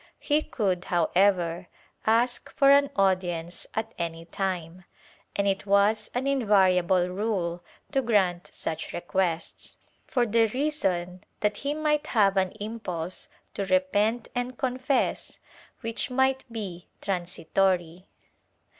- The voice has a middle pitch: No, high, 195 Hz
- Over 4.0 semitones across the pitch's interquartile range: Yes, average, 4.8 semitones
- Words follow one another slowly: Yes, slow, 120 wpm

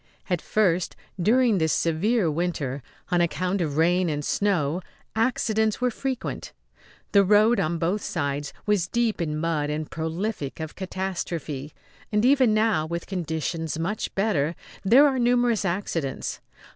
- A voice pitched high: No, medium, 180 Hz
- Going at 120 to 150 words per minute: Yes, average, 140 wpm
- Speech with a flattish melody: No, average, 5.2 semitones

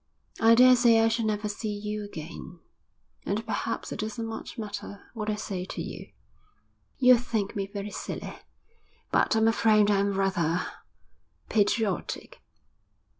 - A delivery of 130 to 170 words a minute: Yes, slow, 135 wpm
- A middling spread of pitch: No, narrow, 2.0 semitones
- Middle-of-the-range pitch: No, high, 210 Hz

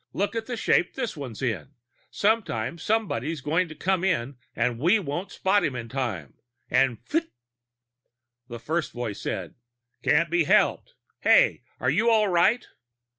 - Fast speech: No, average, 165 wpm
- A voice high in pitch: No, medium, 165 Hz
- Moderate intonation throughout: No, wide, 8.5 semitones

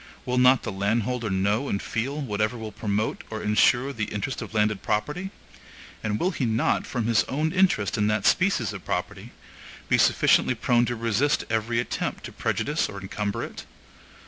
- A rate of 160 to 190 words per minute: Yes, average, 175 wpm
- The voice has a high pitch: No, low, 115 Hz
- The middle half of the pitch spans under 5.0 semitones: Yes, average, 3.3 semitones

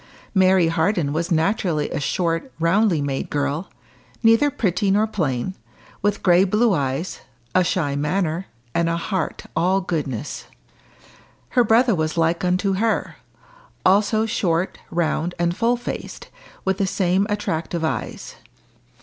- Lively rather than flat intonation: No, average, 3.8 semitones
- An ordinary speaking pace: No, slow, 130 wpm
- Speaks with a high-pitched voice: No, medium, 180 Hz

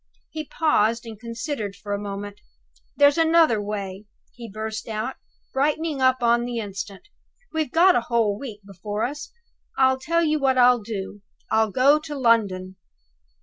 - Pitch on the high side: Yes, high, 235 Hz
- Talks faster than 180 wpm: No, average, 155 wpm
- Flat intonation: No, average, 5.3 semitones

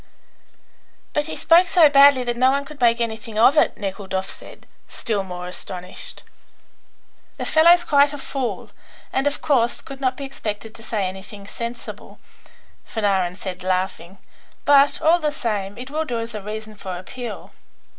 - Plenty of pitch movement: Yes, wide, 6.1 semitones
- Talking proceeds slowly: No, average, 165 wpm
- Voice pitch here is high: Yes, high, 235 Hz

